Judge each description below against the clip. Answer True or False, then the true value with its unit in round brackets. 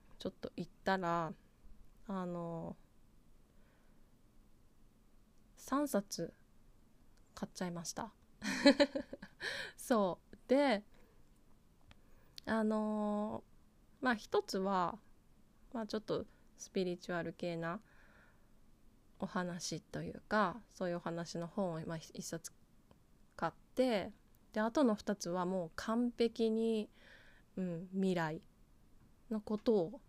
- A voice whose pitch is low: False (190 Hz)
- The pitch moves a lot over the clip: False (4.7 semitones)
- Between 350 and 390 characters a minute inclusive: False (170 characters per minute)